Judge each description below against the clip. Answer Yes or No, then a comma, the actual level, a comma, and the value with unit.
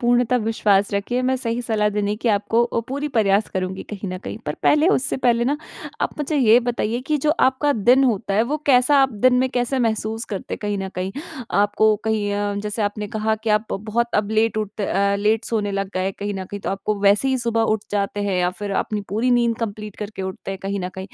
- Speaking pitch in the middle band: No, high, 215 Hz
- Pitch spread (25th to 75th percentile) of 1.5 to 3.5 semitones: Yes, average, 3.2 semitones